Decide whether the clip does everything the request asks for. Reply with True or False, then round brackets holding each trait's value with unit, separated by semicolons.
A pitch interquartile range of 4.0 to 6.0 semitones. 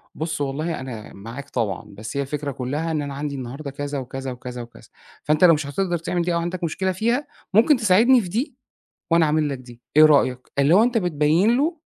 True (5.1 semitones)